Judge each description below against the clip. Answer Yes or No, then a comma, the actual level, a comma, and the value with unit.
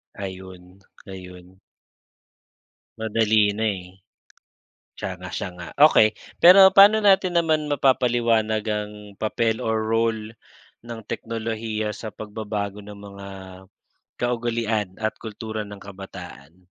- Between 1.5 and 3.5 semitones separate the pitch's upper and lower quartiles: Yes, narrow, 2.5 semitones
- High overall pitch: No, low, 110 Hz